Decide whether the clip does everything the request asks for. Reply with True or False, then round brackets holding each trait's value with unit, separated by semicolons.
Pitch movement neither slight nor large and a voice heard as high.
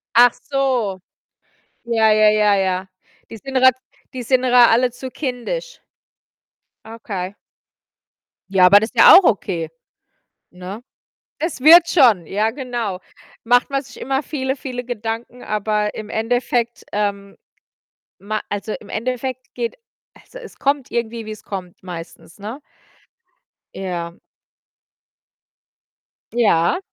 True (3.9 semitones; 230 Hz)